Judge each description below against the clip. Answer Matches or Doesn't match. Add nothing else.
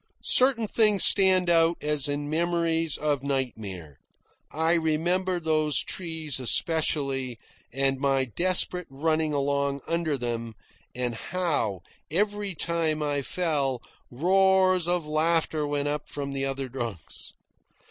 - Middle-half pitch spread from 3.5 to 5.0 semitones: Matches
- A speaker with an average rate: Doesn't match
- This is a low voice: Doesn't match